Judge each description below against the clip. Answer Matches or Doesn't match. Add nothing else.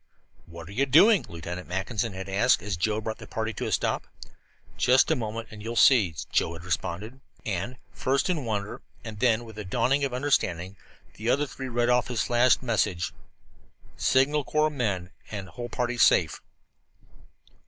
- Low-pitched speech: Matches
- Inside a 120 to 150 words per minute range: Doesn't match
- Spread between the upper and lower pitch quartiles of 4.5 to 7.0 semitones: Matches